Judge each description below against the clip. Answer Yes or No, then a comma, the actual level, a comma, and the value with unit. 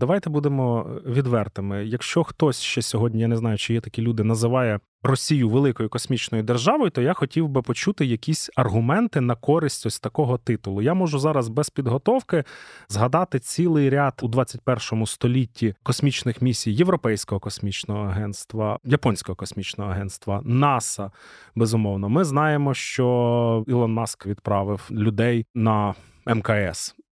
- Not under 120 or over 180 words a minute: Yes, slow, 135 wpm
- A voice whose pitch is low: Yes, low, 120 Hz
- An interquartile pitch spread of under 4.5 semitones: Yes, average, 4.1 semitones